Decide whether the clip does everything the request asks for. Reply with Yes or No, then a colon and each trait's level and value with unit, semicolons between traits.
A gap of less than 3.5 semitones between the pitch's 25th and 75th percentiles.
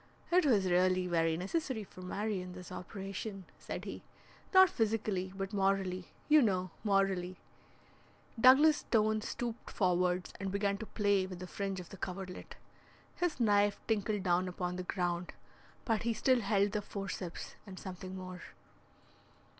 Yes: average, 2.8 semitones